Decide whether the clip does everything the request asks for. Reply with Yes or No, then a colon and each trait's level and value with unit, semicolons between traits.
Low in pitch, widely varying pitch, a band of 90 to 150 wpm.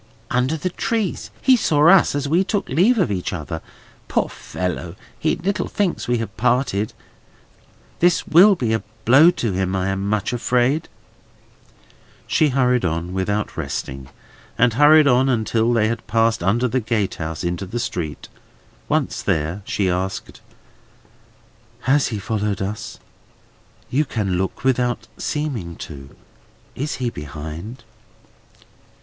Yes: low, 115 Hz; wide, 6.7 semitones; average, 140 wpm